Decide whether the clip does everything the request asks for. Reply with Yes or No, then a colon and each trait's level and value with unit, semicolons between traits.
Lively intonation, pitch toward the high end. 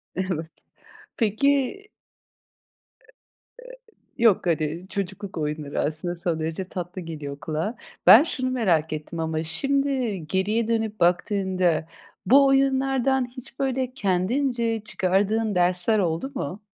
Yes: wide, 6.8 semitones; high, 195 Hz